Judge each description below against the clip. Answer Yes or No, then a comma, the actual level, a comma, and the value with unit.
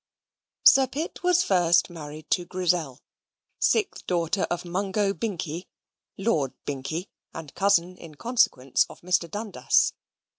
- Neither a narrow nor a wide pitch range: Yes, average, 4.0 semitones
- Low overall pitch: No, medium, 180 Hz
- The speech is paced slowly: Yes, slow, 120 wpm